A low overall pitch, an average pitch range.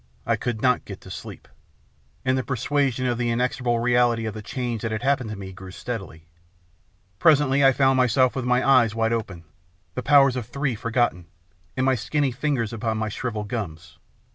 Yes: low, 120 Hz; average, 3.1 semitones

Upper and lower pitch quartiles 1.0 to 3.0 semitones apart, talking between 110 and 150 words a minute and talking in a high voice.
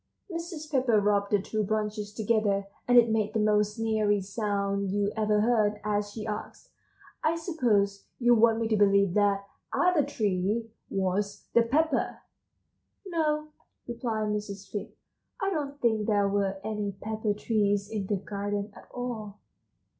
Yes: narrow, 2.4 semitones; average, 145 wpm; high, 210 Hz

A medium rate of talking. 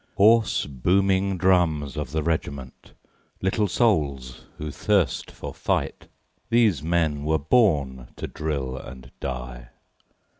No: slow, 115 wpm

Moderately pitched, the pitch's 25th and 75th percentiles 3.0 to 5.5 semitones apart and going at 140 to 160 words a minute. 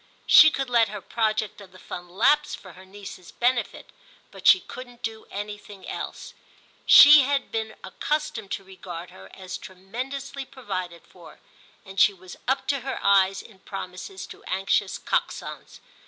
No: high, 205 Hz; average, 5.2 semitones; average, 155 wpm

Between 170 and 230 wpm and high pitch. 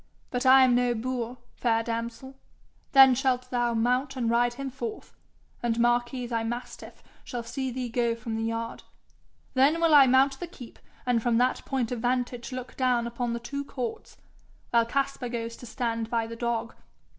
Yes: average, 180 wpm; high, 245 Hz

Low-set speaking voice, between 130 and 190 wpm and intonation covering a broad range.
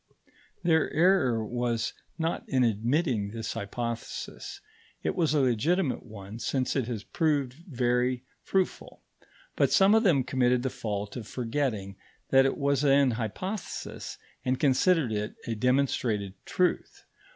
No: low, 125 Hz; slow, 135 wpm; average, 4.5 semitones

